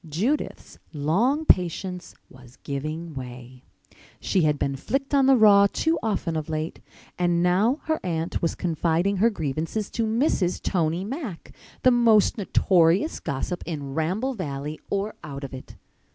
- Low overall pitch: No, medium, 175 Hz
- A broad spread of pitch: Yes, wide, 6.0 semitones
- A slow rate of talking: No, average, 145 wpm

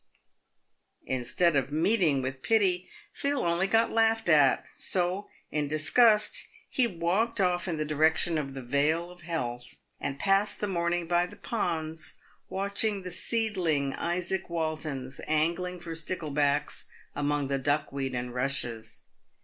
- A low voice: No, medium, 165 Hz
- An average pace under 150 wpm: Yes, average, 140 wpm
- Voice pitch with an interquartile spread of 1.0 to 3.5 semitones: No, average, 4.6 semitones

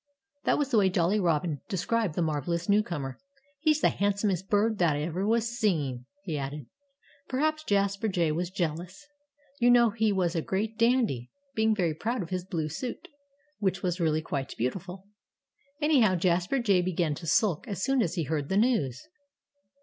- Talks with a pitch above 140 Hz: Yes, medium, 185 Hz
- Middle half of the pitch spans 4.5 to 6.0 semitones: Yes, average, 5.2 semitones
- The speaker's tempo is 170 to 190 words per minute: Yes, average, 175 wpm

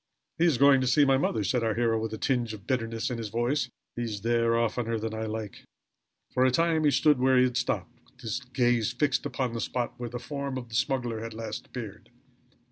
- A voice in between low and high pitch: No, low, 120 Hz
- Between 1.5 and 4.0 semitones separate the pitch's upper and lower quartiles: Yes, narrow, 2.4 semitones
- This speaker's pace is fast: Yes, fast, 235 wpm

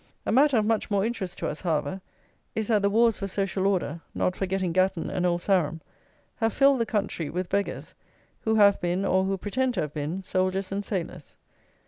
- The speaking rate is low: No, average, 200 wpm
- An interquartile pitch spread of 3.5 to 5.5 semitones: No, average, 2.9 semitones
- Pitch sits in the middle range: No, high, 195 Hz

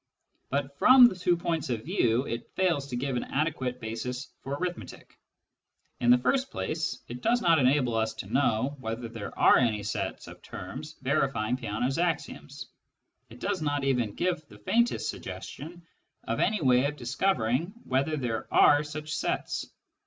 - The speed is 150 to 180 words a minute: Yes, average, 160 wpm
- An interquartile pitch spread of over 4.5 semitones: Yes, average, 5.1 semitones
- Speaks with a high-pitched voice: No, low, 135 Hz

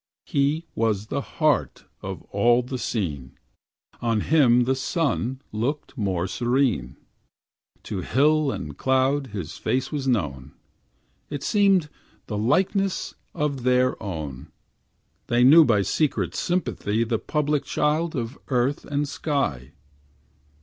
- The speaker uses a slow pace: Yes, slow, 120 wpm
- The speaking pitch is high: No, low, 130 Hz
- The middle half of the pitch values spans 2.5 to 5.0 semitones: No, wide, 5.5 semitones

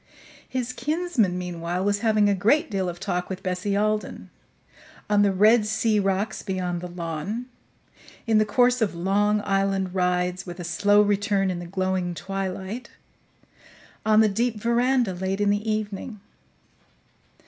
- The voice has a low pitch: No, high, 200 Hz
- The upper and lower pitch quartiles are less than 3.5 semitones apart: Yes, average, 2.7 semitones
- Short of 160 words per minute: Yes, average, 150 wpm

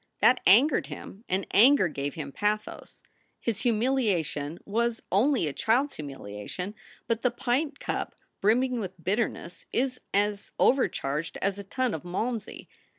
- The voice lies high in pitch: Yes, high, 210 Hz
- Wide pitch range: Yes, wide, 5.8 semitones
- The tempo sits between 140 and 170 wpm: Yes, average, 145 wpm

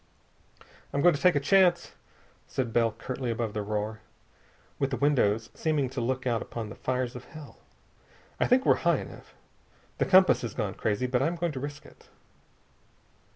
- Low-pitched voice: Yes, low, 130 Hz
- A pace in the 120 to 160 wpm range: No, average, 180 wpm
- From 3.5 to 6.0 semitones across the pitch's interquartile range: Yes, average, 4.5 semitones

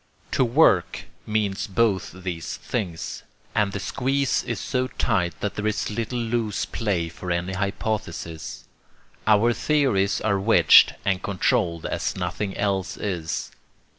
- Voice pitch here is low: Yes, low, 100 Hz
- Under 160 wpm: Yes, slow, 135 wpm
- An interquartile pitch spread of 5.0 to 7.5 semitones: No, average, 3.7 semitones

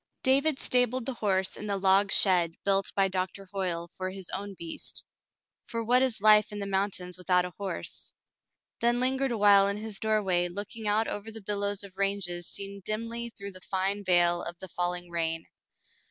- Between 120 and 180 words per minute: No, average, 190 wpm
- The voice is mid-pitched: No, high, 200 Hz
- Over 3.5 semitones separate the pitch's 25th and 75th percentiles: No, average, 2.7 semitones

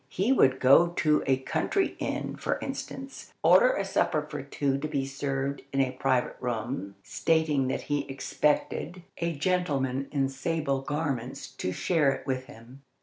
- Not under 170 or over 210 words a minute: No, average, 160 wpm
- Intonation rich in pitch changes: No, average, 3.3 semitones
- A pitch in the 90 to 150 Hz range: Yes, medium, 140 Hz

